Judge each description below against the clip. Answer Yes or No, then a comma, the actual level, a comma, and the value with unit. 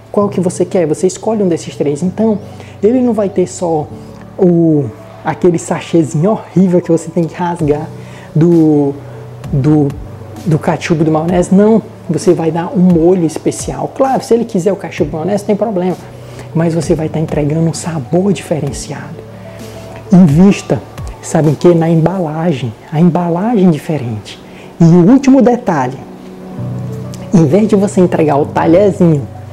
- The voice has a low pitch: No, medium, 165 Hz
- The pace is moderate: Yes, average, 150 wpm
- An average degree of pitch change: Yes, average, 4.4 semitones